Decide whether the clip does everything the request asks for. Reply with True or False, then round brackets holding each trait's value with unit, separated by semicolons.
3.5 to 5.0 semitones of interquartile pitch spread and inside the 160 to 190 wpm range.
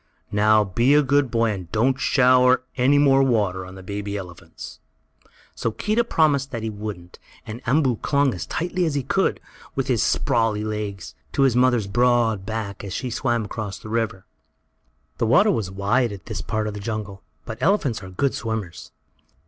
True (4.2 semitones; 180 wpm)